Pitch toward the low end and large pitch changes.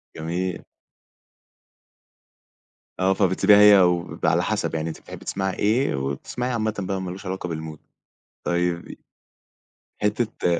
No: very low, 95 Hz; average, 3.1 semitones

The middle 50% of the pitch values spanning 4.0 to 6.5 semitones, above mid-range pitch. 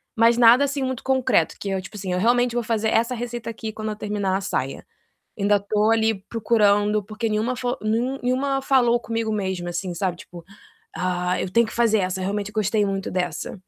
No: average, 3.4 semitones; high, 215 Hz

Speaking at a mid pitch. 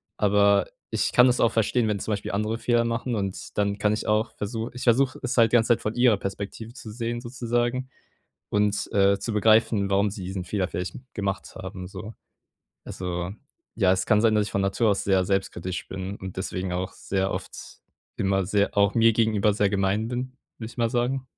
No: low, 105 Hz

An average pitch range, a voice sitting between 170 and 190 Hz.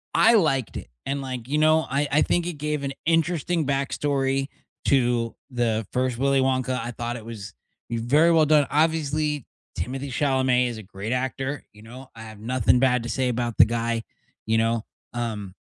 No: average, 3.6 semitones; low, 130 Hz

